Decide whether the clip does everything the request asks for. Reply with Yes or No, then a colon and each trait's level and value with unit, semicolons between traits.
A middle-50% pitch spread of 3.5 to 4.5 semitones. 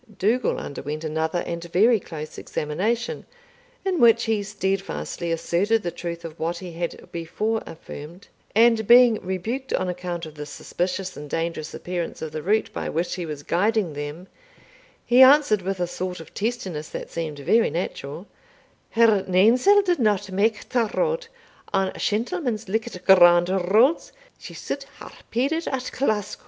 No: average, 5.2 semitones